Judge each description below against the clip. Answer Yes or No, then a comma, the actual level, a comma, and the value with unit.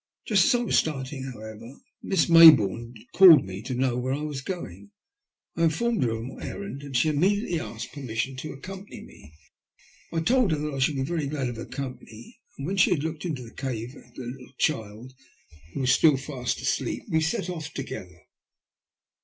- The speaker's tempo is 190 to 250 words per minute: Yes, fast, 205 wpm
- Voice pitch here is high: No, medium, 140 Hz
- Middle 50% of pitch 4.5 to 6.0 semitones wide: Yes, average, 4.8 semitones